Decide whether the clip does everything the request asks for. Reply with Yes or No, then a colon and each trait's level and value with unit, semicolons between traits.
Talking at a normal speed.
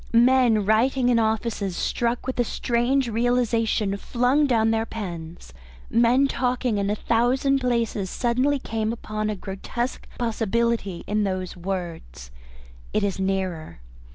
No: slow, 130 wpm